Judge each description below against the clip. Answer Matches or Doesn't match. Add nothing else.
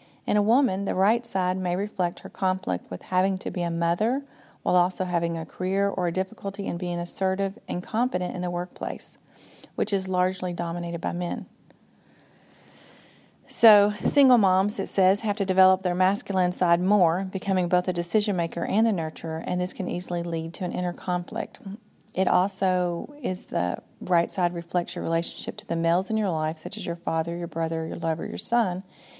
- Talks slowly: Doesn't match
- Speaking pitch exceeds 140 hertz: Matches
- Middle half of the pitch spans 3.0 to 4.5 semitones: Doesn't match